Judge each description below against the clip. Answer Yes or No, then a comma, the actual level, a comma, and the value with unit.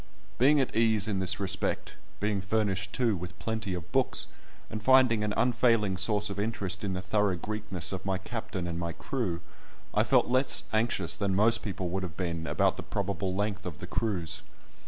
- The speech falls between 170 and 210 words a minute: Yes, average, 190 wpm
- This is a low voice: Yes, low, 100 Hz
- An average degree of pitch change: Yes, average, 3.2 semitones